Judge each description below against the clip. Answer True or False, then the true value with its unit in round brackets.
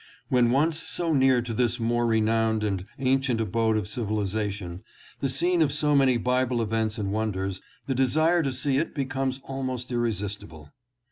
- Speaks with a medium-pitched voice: False (120 Hz)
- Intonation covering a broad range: False (3.7 semitones)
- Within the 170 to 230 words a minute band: False (160 wpm)